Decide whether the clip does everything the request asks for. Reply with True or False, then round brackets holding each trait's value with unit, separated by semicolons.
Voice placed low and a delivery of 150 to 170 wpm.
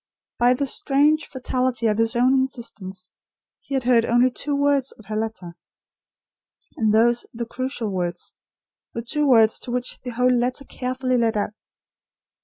False (245 Hz; 160 wpm)